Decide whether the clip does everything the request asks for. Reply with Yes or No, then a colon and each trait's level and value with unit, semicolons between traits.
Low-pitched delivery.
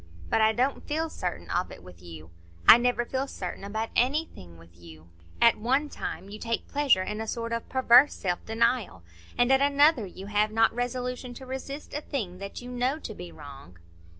No: high, 230 Hz